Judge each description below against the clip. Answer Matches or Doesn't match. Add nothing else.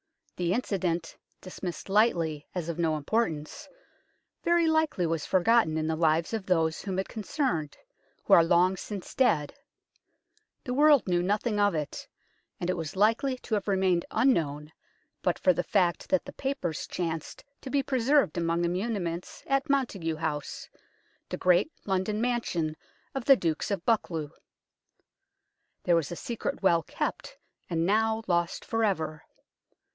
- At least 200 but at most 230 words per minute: Doesn't match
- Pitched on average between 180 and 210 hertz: Matches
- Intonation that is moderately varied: Doesn't match